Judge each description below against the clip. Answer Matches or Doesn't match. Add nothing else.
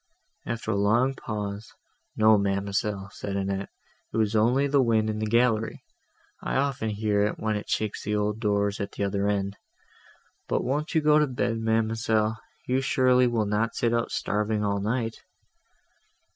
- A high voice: Doesn't match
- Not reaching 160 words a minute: Doesn't match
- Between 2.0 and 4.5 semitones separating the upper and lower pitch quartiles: Matches